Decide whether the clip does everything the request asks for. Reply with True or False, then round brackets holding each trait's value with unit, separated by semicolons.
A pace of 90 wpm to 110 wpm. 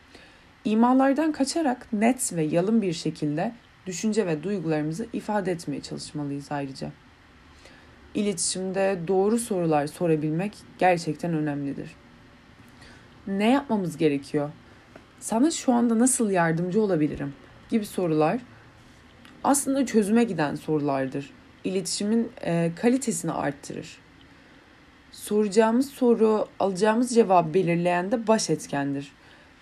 True (95 wpm)